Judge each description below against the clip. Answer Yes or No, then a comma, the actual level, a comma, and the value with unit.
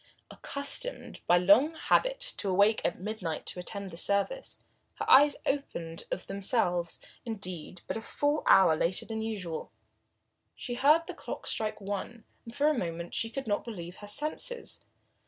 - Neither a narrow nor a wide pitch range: No, wide, 7.1 semitones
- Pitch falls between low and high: No, high, 210 Hz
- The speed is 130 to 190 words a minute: Yes, average, 155 wpm